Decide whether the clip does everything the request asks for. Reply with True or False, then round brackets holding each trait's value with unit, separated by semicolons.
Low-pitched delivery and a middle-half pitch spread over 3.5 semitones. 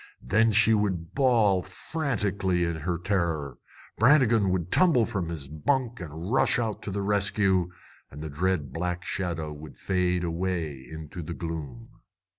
True (90 Hz; 4.2 semitones)